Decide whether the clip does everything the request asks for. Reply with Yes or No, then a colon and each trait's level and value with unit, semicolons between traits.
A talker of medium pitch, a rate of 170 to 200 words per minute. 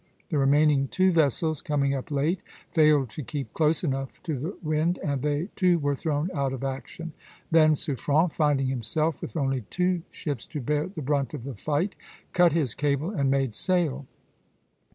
Yes: medium, 150 Hz; average, 185 wpm